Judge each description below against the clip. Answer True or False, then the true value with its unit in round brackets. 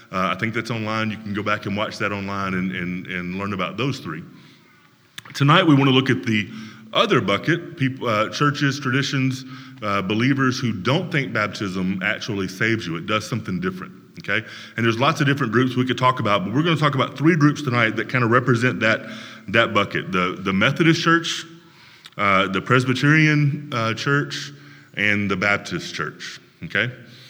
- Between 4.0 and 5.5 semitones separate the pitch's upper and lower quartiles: True (5.1 semitones)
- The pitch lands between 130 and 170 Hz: False (120 Hz)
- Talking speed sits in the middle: True (190 wpm)